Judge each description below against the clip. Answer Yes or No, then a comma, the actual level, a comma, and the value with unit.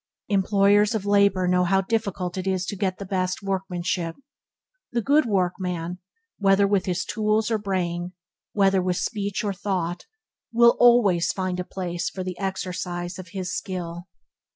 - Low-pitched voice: No, high, 190 Hz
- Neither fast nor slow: Yes, average, 150 wpm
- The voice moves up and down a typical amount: No, narrow, 2.0 semitones